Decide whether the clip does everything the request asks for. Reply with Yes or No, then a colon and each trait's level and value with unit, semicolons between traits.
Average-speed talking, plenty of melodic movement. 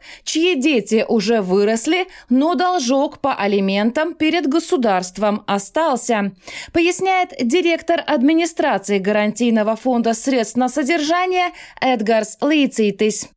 No: slow, 95 wpm; wide, 7.4 semitones